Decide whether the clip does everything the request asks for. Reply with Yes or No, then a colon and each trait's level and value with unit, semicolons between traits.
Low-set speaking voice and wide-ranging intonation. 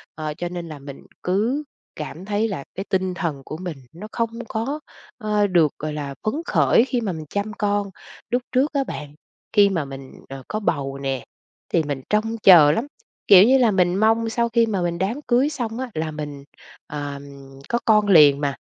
No: high, 190 Hz; wide, 6.8 semitones